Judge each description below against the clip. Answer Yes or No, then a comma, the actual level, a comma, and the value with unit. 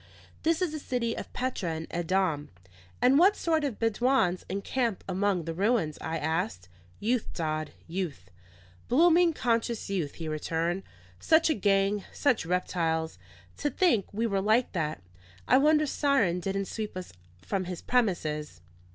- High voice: Yes, high, 195 Hz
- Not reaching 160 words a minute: Yes, average, 150 wpm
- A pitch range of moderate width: No, wide, 7.0 semitones